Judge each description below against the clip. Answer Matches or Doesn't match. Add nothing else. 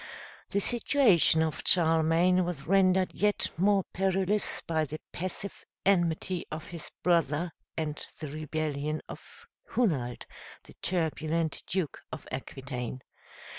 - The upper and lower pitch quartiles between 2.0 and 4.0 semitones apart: Matches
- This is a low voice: Doesn't match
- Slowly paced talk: Matches